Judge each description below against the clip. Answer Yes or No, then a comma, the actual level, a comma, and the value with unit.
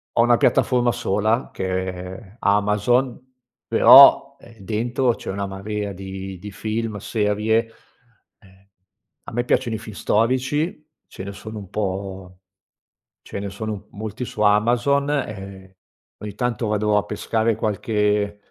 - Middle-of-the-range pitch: No, low, 105 Hz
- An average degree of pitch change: Yes, average, 3.1 semitones